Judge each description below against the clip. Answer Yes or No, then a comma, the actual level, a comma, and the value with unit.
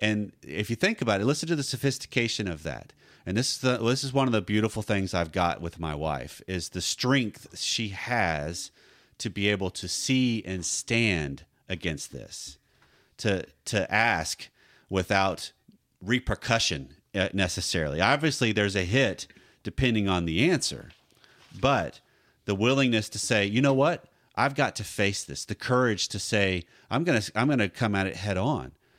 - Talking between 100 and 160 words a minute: No, average, 170 wpm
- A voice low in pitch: Yes, low, 105 Hz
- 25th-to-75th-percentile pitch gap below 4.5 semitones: No, average, 4.8 semitones